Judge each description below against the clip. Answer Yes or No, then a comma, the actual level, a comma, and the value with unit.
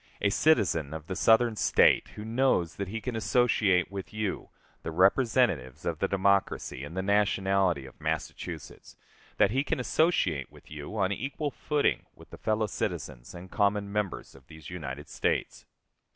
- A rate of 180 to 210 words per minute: No, average, 165 wpm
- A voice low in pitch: Yes, low, 100 Hz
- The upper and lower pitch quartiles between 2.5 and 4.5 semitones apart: No, average, 5.1 semitones